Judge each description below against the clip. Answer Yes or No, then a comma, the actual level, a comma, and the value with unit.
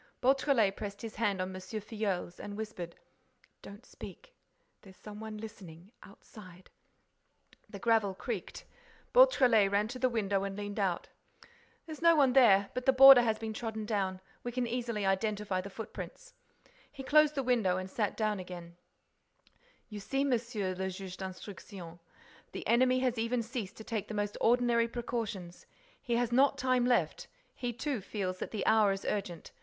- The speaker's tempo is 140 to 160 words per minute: Yes, average, 155 wpm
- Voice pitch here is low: No, high, 215 Hz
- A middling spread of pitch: Yes, average, 3.9 semitones